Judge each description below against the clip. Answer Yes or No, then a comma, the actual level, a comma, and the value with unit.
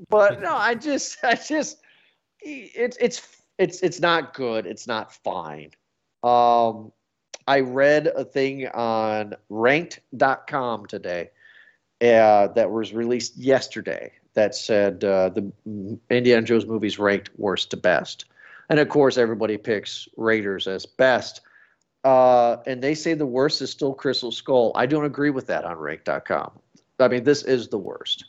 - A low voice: Yes, low, 125 Hz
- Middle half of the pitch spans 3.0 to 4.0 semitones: No, average, 4.8 semitones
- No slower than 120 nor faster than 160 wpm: Yes, average, 150 wpm